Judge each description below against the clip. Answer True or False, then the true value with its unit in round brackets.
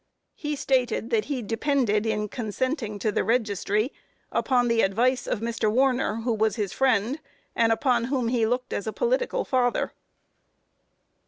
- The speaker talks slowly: False (155 wpm)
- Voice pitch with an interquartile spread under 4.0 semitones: True (3.1 semitones)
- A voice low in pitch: False (235 Hz)